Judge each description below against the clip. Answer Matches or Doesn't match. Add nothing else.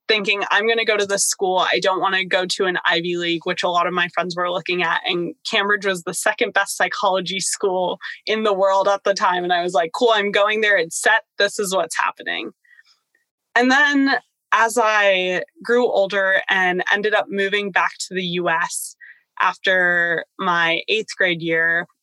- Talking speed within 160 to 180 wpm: Doesn't match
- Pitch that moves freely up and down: Doesn't match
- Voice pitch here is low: Doesn't match